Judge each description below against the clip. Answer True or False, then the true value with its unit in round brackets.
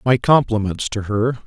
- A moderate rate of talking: True (165 wpm)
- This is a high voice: False (115 Hz)